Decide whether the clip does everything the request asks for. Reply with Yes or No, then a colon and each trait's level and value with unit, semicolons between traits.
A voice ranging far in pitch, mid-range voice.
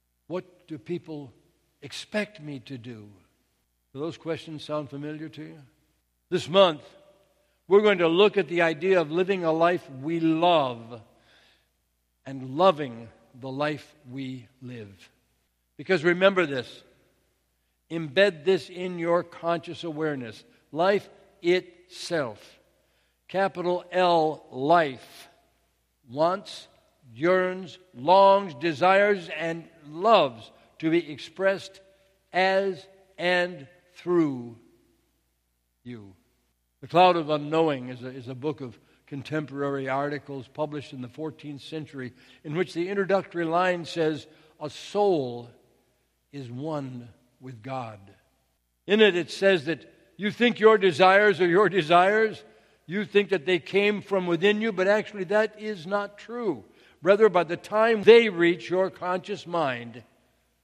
Yes: wide, 6.1 semitones; medium, 160 Hz